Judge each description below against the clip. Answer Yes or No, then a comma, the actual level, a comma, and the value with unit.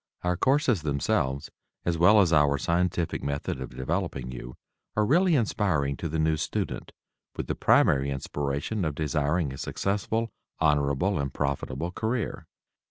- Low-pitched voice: Yes, very low, 80 Hz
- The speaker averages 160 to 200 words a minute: No, average, 145 wpm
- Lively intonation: Yes, wide, 5.7 semitones